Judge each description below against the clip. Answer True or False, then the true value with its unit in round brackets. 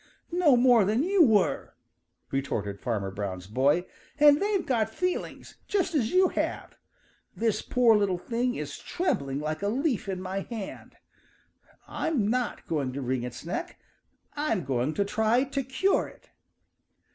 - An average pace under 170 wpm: True (150 wpm)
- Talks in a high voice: True (215 Hz)